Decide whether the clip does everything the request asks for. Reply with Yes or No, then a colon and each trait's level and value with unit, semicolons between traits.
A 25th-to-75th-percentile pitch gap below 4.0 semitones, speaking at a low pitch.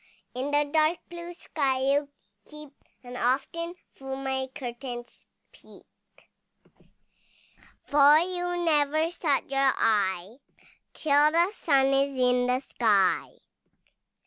No: average, 3.5 semitones; very high, 275 Hz